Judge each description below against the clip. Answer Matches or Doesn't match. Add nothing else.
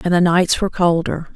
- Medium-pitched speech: Matches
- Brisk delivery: Matches